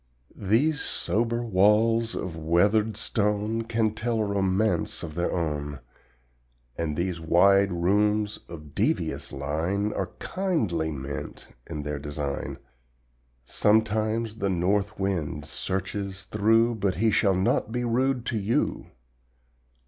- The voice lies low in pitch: Yes, low, 100 Hz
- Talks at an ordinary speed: No, slow, 120 wpm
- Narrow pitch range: No, average, 4.5 semitones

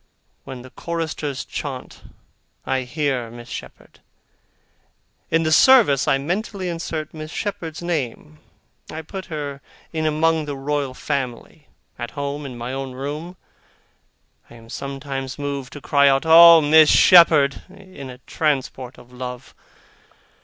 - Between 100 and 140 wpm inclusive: Yes, slow, 135 wpm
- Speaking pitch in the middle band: Yes, medium, 145 Hz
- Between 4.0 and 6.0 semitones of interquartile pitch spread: No, average, 3.3 semitones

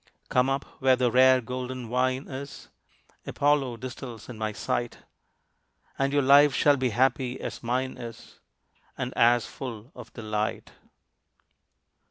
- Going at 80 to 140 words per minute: Yes, slow, 135 wpm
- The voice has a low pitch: Yes, low, 125 Hz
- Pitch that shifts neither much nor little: No, narrow, 1.9 semitones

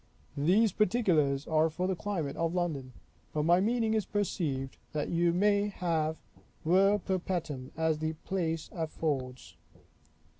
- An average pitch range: Yes, average, 3.8 semitones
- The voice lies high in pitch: No, medium, 170 Hz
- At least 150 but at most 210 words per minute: No, slow, 135 wpm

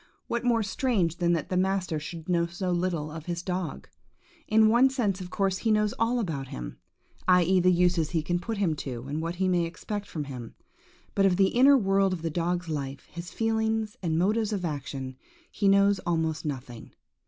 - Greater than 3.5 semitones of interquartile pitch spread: Yes, average, 3.9 semitones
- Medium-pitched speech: Yes, medium, 180 Hz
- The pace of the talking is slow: No, average, 200 wpm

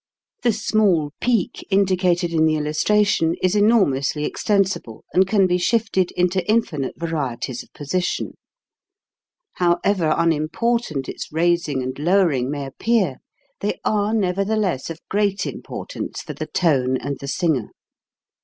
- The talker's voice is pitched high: No, medium, 175 Hz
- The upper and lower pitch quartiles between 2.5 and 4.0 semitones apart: No, average, 5.1 semitones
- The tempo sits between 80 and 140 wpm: Yes, slow, 135 wpm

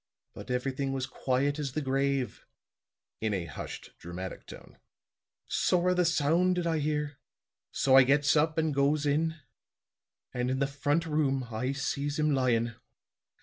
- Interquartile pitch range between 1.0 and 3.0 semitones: Yes, average, 2.7 semitones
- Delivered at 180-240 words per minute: No, average, 150 wpm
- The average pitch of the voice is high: No, medium, 140 Hz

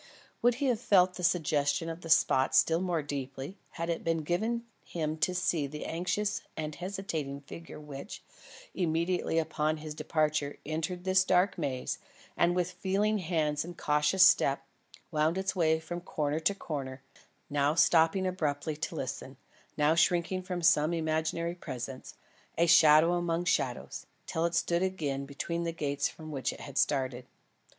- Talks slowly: No, average, 160 wpm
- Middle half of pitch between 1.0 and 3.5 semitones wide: Yes, average, 3.1 semitones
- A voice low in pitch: No, medium, 165 Hz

